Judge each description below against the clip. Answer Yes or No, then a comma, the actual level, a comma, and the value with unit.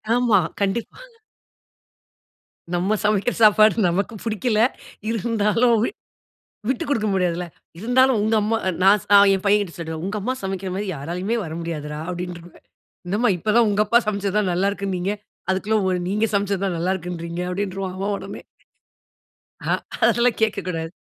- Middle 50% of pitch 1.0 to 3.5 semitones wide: Yes, average, 3.1 semitones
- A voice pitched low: No, high, 200 Hz